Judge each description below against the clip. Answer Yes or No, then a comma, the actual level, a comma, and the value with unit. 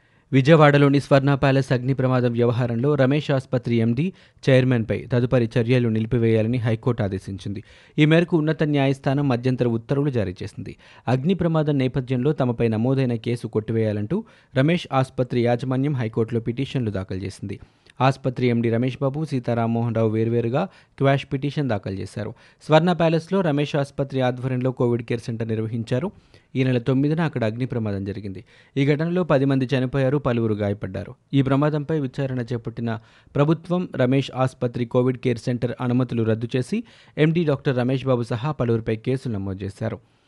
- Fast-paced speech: Yes, fast, 140 wpm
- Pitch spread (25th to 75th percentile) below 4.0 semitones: Yes, average, 3.2 semitones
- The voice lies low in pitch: Yes, low, 130 Hz